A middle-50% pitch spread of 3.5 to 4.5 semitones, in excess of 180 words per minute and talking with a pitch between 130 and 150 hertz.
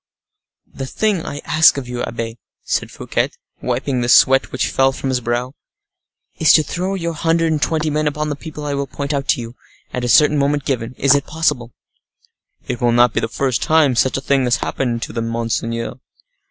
Yes: average, 3.8 semitones; fast, 205 wpm; low, 135 Hz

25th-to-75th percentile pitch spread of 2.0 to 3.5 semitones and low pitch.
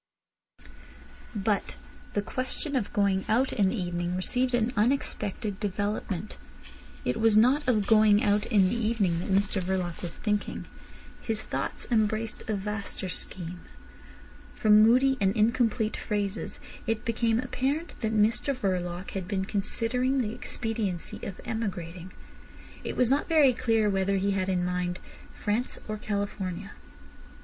No: average, 3.2 semitones; high, 210 Hz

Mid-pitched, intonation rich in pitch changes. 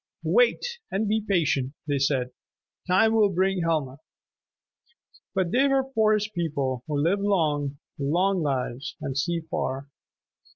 Yes: medium, 170 Hz; wide, 6.4 semitones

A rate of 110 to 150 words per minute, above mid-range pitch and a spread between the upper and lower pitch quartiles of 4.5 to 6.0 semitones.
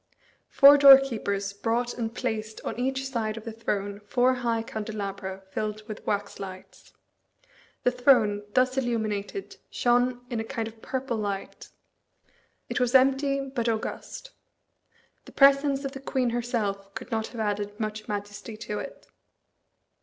No: average, 145 wpm; high, 230 Hz; average, 3.5 semitones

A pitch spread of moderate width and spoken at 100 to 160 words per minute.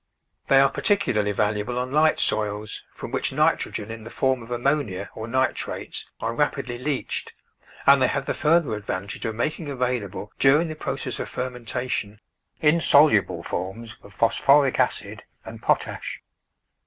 Yes: average, 4.6 semitones; average, 150 wpm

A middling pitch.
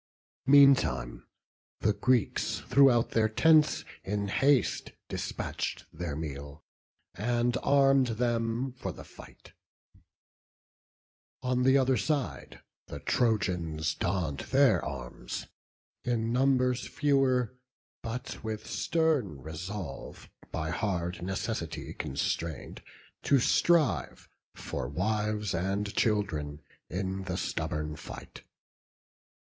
No: low, 110 Hz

